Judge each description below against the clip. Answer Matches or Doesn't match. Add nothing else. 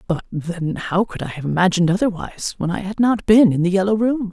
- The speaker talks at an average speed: Doesn't match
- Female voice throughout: Matches